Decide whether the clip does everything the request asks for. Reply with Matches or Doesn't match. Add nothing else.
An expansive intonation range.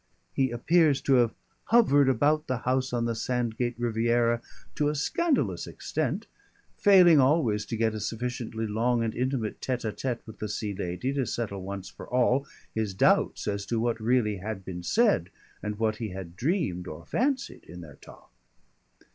Doesn't match